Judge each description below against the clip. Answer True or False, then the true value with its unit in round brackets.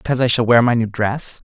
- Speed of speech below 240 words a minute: False (285 wpm)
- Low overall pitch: True (120 Hz)